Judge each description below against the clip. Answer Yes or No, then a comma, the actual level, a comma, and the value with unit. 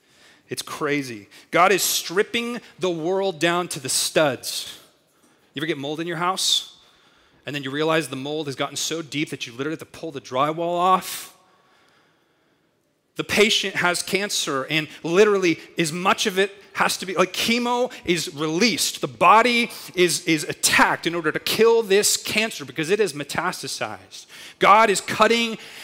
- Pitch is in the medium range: Yes, medium, 170 Hz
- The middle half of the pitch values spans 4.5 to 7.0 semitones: Yes, average, 4.9 semitones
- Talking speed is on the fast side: No, average, 165 wpm